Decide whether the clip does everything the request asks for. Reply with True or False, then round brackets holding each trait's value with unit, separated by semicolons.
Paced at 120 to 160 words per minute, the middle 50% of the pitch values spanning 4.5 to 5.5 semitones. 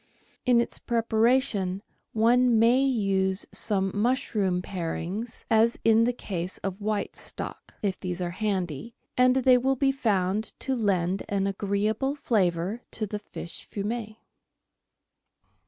False (135 wpm; 3.8 semitones)